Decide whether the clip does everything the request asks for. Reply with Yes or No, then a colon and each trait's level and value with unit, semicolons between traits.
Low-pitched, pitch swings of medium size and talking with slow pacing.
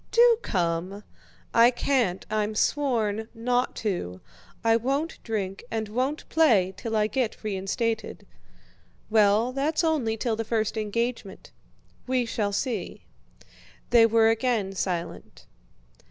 No: high, 225 Hz; average, 3.4 semitones; slow, 120 wpm